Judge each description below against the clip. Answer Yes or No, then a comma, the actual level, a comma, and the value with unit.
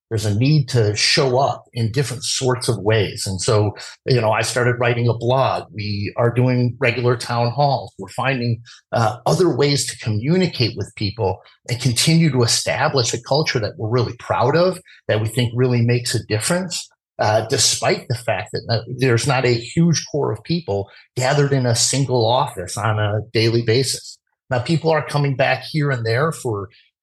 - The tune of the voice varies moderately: Yes, average, 3.4 semitones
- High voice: No, low, 120 Hz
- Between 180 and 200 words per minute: Yes, average, 185 wpm